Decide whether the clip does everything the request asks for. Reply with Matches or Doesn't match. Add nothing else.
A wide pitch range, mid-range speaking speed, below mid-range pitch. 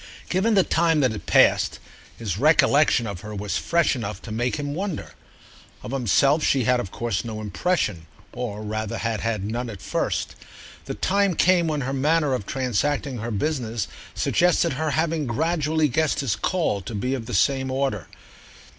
Matches